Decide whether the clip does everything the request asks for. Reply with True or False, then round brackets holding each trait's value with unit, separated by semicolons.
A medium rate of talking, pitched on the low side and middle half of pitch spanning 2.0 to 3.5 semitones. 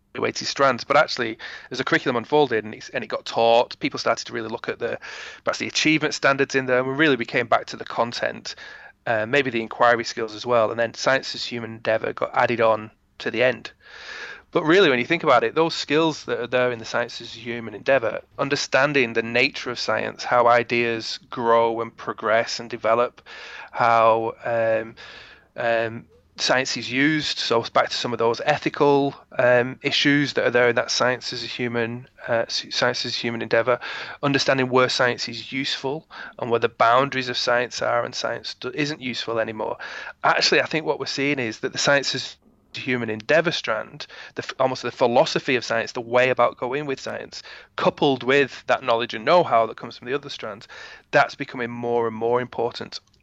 True (195 wpm; 120 Hz; 2.9 semitones)